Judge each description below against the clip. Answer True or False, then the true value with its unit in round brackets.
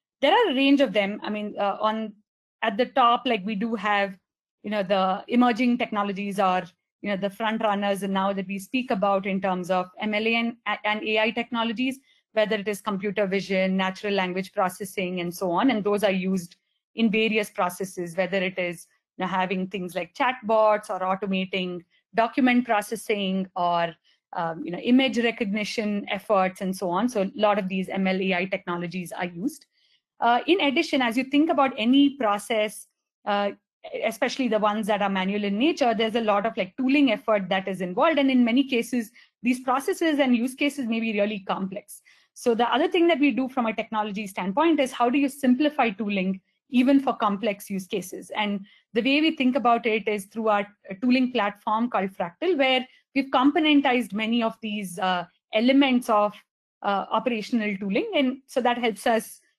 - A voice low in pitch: False (215 Hz)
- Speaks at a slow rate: False (190 wpm)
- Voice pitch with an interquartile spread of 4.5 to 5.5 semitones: False (4.1 semitones)